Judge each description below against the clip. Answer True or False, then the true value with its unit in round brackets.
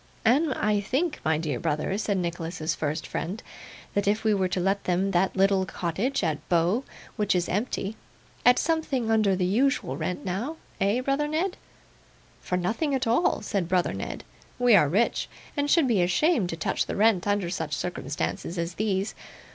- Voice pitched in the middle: False (195 Hz)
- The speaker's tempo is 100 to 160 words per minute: False (180 wpm)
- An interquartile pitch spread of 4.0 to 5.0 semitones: False (5.5 semitones)